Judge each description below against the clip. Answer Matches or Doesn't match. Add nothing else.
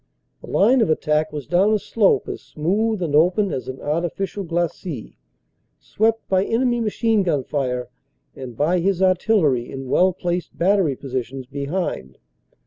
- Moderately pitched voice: Matches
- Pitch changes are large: Matches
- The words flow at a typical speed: Matches